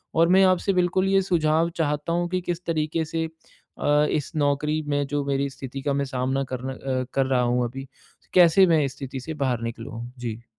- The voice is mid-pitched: Yes, medium, 145 Hz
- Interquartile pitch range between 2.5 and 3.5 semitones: No, average, 3.9 semitones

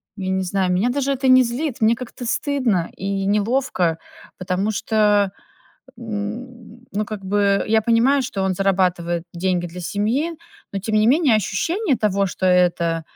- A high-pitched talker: Yes, high, 205 Hz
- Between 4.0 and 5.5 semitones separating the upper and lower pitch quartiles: Yes, average, 4.3 semitones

